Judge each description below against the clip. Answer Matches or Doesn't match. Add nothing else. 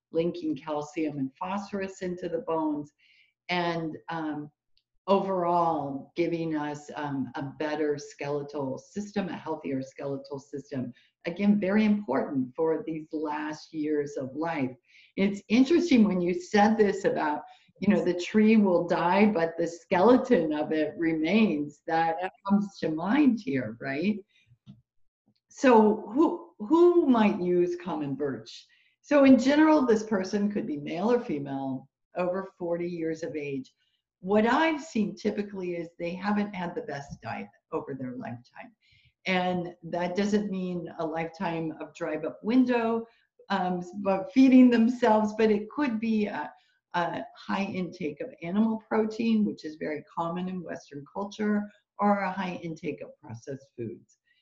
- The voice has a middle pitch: Matches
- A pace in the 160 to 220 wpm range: Doesn't match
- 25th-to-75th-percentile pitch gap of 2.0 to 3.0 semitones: Doesn't match